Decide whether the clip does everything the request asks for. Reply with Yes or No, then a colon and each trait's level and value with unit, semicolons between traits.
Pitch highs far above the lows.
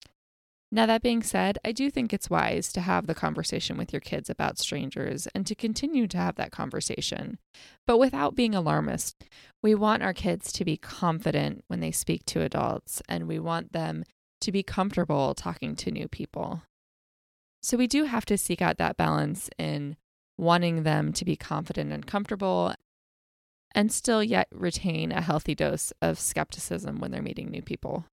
Yes: wide, 6.4 semitones